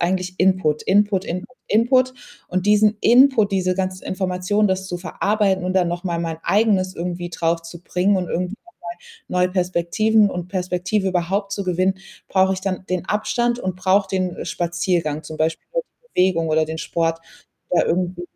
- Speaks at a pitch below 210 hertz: Yes, medium, 185 Hz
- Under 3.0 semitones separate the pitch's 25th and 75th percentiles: Yes, narrow, 2.4 semitones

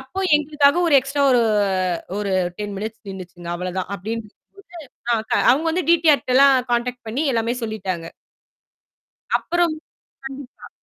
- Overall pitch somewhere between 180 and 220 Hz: No, high, 240 Hz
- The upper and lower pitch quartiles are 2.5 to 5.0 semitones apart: No, wide, 5.5 semitones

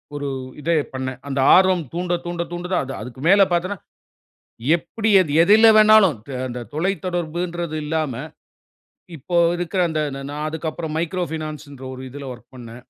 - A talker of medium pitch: Yes, medium, 160 Hz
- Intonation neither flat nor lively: Yes, average, 4.0 semitones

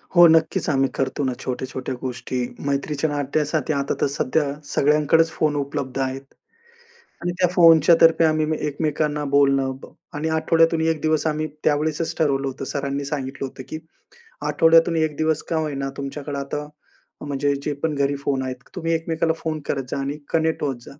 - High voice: No, medium, 145 Hz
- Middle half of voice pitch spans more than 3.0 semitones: No, narrow, 2.5 semitones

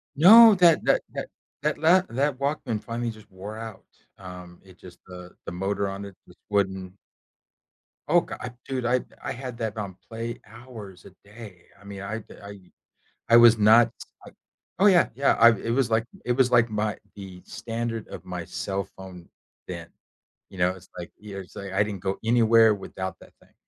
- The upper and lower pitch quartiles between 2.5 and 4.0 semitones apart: Yes, average, 3.6 semitones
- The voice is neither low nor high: No, low, 110 Hz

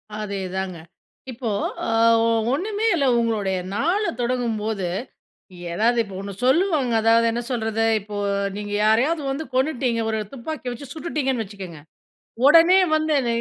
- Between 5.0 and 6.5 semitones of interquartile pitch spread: Yes, wide, 5.4 semitones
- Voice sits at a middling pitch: No, high, 235 Hz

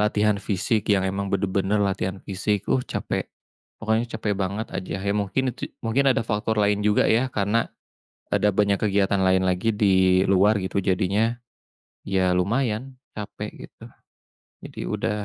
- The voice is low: Yes, low, 100 Hz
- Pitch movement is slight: Yes, narrow, 2.2 semitones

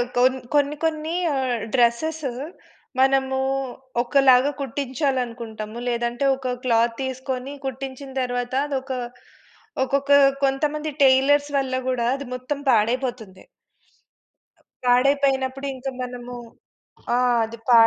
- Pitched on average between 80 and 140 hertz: No, very high, 260 Hz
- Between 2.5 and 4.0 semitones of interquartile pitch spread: No, narrow, 2.0 semitones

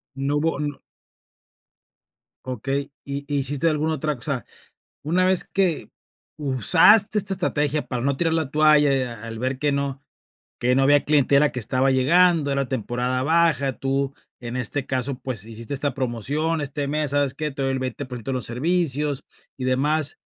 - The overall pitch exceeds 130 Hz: Yes, medium, 140 Hz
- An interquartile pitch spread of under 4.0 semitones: Yes, average, 2.8 semitones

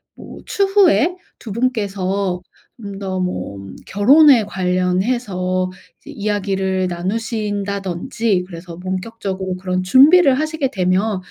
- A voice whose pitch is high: Yes, high, 200 Hz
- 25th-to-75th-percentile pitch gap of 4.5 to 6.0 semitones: No, average, 4.1 semitones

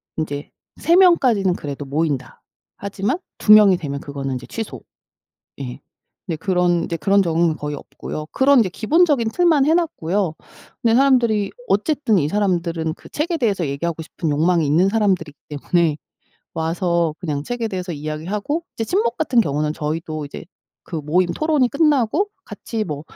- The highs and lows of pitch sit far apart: Yes, wide, 7.0 semitones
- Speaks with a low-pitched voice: No, medium, 180 Hz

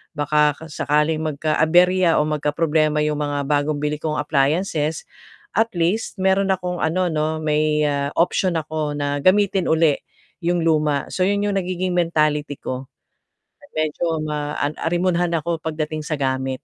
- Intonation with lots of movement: No, average, 2.8 semitones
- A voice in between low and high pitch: Yes, medium, 155 Hz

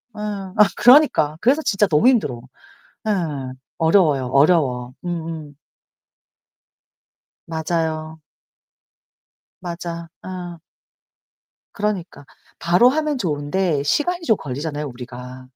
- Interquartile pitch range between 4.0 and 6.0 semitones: Yes, wide, 5.5 semitones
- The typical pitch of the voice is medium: Yes, medium, 165 Hz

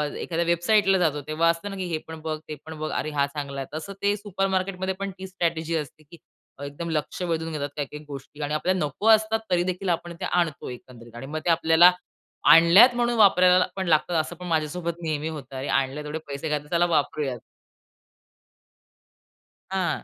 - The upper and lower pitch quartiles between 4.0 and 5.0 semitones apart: No, average, 3.5 semitones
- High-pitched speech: No, medium, 165 Hz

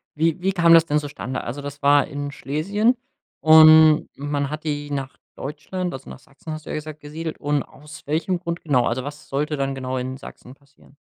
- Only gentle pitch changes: Yes, narrow, 2.1 semitones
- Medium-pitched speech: Yes, medium, 150 Hz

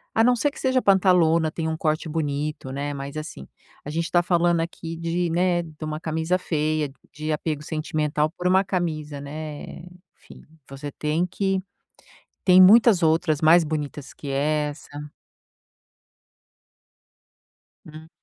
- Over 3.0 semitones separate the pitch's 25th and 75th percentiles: No, narrow, 2.5 semitones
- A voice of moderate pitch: Yes, medium, 160 Hz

